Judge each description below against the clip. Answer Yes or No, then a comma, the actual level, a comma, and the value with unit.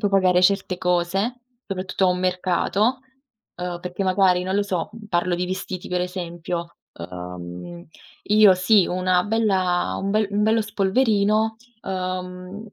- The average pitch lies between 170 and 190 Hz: Yes, medium, 185 Hz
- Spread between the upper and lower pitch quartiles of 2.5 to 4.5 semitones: No, narrow, 2.1 semitones